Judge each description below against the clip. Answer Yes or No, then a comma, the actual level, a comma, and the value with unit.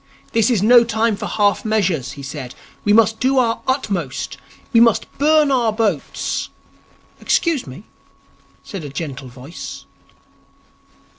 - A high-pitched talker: Yes, high, 215 Hz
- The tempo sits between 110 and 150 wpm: Yes, average, 140 wpm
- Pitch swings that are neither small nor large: No, wide, 6.8 semitones